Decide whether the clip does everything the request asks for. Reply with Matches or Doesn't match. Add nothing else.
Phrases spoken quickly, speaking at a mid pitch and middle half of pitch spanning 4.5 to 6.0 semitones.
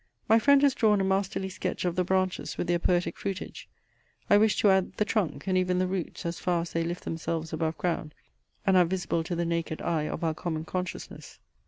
Doesn't match